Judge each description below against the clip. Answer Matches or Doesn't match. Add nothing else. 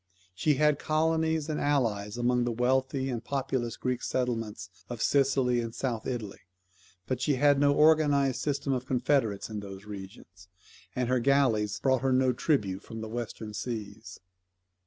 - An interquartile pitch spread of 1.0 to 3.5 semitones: Doesn't match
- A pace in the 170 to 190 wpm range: Doesn't match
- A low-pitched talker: Matches